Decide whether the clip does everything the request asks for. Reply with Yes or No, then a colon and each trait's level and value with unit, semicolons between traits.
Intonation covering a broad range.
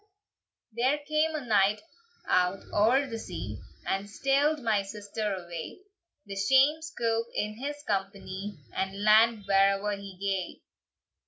No: average, 4.5 semitones